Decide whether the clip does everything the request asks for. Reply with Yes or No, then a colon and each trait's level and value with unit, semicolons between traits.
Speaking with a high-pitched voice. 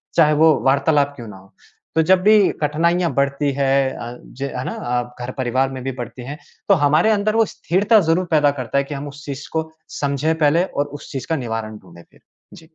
No: medium, 145 Hz